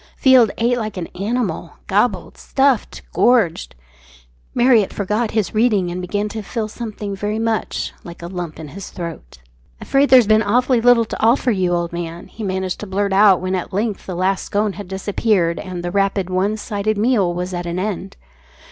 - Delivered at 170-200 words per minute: Yes, average, 185 wpm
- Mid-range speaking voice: No, high, 200 Hz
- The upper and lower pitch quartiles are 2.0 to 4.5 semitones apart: Yes, average, 3.5 semitones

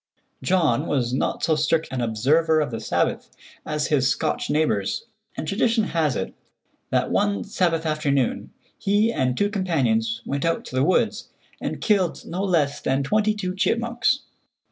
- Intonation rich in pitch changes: Yes, wide, 6.8 semitones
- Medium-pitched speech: Yes, medium, 160 Hz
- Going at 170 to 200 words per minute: No, average, 160 wpm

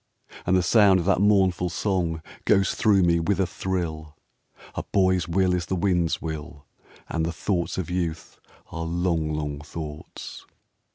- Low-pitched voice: Yes, very low, 85 Hz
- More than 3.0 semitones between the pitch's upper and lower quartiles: No, narrow, 2.6 semitones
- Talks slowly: No, average, 160 wpm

